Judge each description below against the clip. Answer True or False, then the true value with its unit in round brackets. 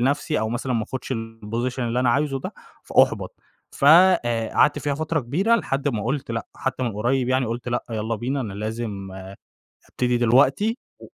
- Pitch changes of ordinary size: True (3.3 semitones)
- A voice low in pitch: True (125 Hz)